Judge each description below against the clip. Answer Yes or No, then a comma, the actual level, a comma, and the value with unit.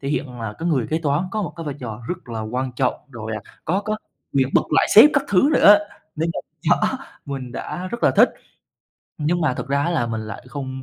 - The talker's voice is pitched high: No, medium, 140 Hz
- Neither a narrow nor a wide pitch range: No, wide, 5.8 semitones